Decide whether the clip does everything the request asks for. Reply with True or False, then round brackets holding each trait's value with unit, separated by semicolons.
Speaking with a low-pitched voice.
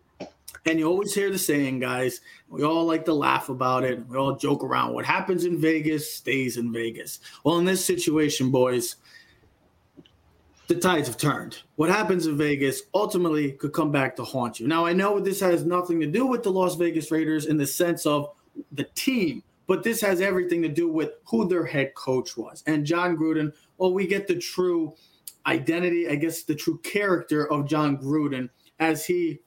False (160 Hz)